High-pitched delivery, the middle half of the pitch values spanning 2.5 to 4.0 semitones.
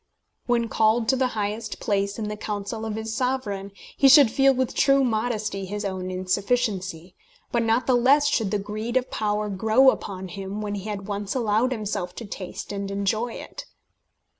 Yes: high, 215 Hz; average, 3.4 semitones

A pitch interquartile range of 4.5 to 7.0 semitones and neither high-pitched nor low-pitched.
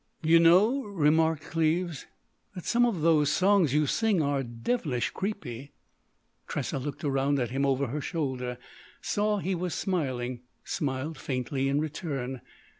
Yes: average, 4.8 semitones; medium, 150 Hz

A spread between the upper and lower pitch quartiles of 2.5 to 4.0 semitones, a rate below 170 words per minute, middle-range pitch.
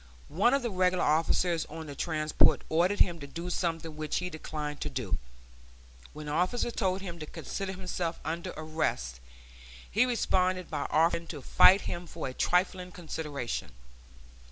Yes: average, 2.8 semitones; average, 160 wpm; medium, 170 Hz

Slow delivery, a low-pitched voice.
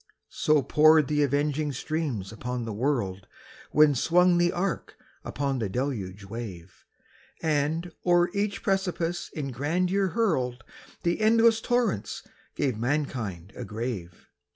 No: slow, 125 wpm; medium, 145 Hz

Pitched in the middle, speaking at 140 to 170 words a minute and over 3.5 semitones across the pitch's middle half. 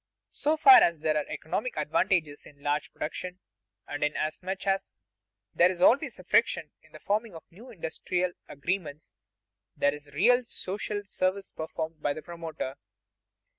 Yes: medium, 175 Hz; average, 150 wpm; average, 4.6 semitones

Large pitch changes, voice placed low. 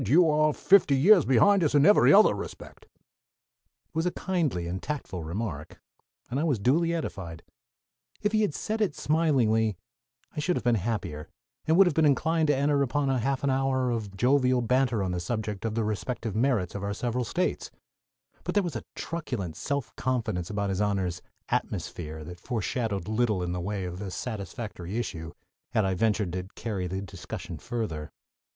Yes: wide, 6.8 semitones; low, 115 Hz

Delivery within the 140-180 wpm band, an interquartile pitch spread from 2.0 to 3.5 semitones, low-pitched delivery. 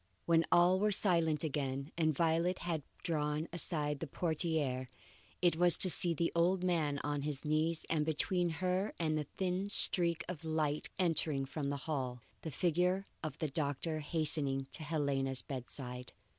No: average, 160 wpm; average, 3.1 semitones; medium, 160 Hz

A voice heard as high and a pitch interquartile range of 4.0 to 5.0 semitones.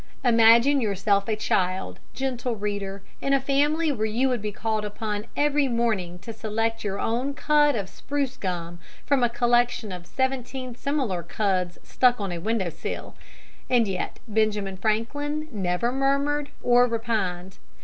Yes: high, 225 Hz; average, 4.7 semitones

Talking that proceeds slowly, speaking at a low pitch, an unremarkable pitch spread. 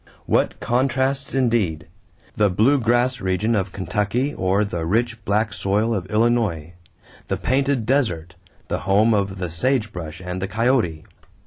No: average, 145 wpm; low, 105 Hz; average, 4.6 semitones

